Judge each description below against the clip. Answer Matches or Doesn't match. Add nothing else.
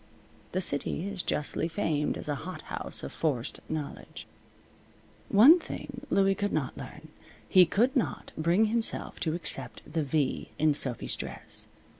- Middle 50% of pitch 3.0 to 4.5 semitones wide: Doesn't match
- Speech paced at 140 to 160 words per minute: Matches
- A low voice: Doesn't match